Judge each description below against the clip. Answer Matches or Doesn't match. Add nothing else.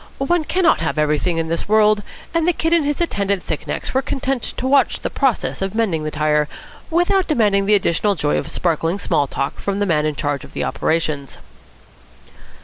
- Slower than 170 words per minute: Doesn't match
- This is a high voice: Matches